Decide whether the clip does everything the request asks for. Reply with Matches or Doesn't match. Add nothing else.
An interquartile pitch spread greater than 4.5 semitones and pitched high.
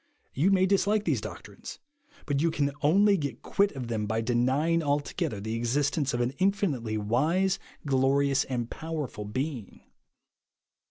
Doesn't match